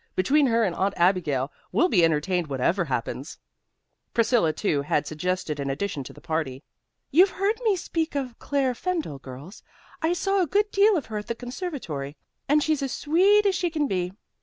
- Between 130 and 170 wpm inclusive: No, average, 185 wpm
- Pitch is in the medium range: No, high, 225 Hz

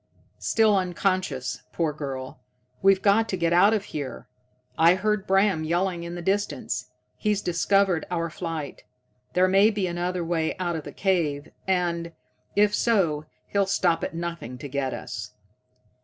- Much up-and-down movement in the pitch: No, average, 3.0 semitones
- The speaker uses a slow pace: No, average, 155 wpm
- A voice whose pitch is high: No, medium, 175 Hz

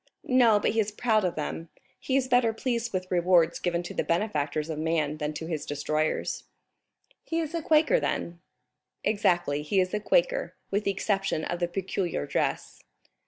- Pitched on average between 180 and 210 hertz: Yes, medium, 185 Hz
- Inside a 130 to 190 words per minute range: Yes, average, 180 wpm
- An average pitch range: No, wide, 5.7 semitones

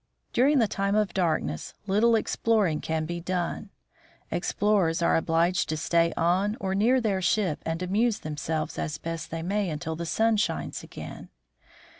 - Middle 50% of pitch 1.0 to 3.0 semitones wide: No, average, 4.4 semitones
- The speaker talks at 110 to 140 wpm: No, average, 160 wpm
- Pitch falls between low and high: Yes, medium, 180 Hz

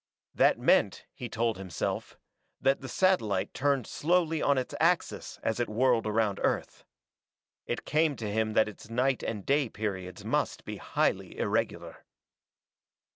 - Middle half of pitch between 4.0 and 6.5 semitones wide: Yes, average, 4.4 semitones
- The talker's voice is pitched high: No, low, 120 Hz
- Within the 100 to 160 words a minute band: Yes, average, 145 wpm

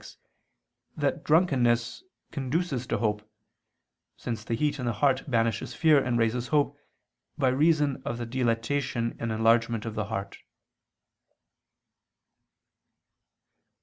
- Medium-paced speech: No, slow, 115 wpm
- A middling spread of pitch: Yes, average, 3.5 semitones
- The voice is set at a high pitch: No, low, 120 Hz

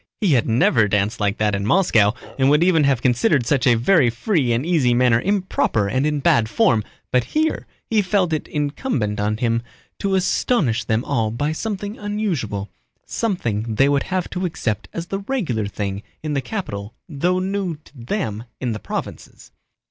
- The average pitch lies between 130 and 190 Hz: Yes, low, 135 Hz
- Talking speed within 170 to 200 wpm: Yes, average, 180 wpm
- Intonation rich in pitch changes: Yes, wide, 8.5 semitones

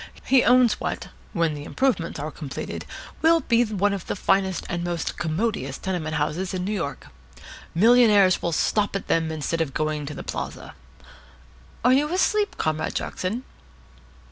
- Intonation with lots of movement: Yes, wide, 6.7 semitones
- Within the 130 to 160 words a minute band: Yes, average, 150 wpm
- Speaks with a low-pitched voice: No, medium, 185 Hz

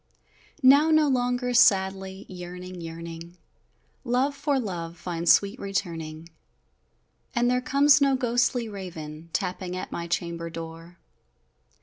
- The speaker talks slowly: Yes, slow, 115 wpm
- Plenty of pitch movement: Yes, wide, 6.7 semitones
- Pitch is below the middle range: No, high, 190 Hz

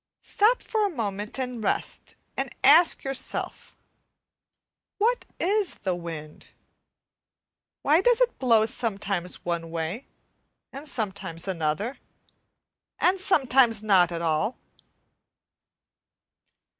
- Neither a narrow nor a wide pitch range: No, wide, 9.0 semitones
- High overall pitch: Yes, high, 225 Hz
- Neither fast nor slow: No, slow, 100 wpm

